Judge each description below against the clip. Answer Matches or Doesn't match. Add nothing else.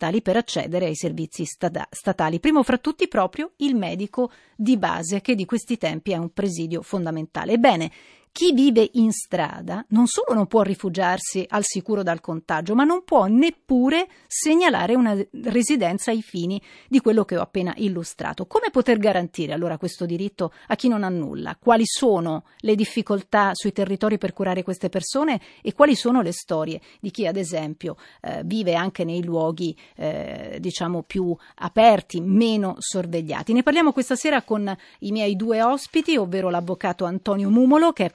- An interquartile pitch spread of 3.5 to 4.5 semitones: Doesn't match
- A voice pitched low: Doesn't match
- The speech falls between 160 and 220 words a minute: Matches